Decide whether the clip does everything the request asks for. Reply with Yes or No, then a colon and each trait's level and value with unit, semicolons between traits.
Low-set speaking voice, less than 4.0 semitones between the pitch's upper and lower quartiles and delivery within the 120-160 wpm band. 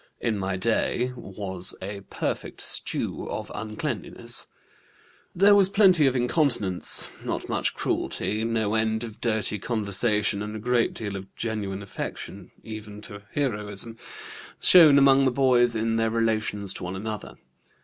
Yes: low, 110 Hz; average, 3.1 semitones; average, 140 wpm